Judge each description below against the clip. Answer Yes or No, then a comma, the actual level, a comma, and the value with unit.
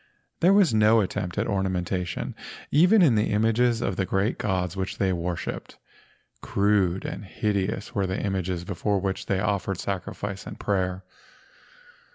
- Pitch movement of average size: No, narrow, 2.2 semitones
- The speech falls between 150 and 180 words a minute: Yes, average, 155 wpm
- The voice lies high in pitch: No, low, 100 Hz